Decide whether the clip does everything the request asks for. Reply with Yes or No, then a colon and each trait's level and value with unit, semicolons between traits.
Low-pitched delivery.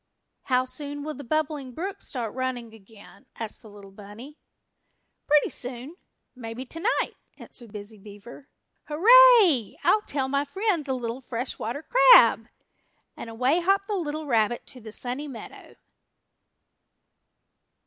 No: very high, 260 Hz